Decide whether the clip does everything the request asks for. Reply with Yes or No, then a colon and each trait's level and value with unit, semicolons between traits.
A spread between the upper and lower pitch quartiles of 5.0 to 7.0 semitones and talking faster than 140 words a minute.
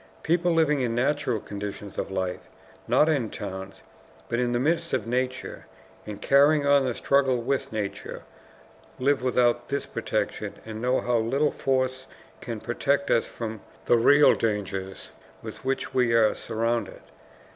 No: average, 3.8 semitones; average, 150 wpm